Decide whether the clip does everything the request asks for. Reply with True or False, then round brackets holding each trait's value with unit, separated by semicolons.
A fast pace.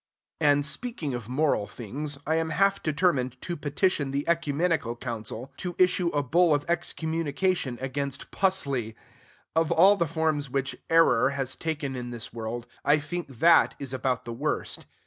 False (160 wpm)